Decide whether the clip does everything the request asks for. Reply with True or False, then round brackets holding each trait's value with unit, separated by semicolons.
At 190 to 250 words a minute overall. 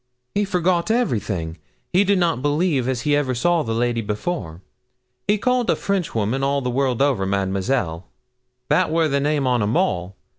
False (175 wpm)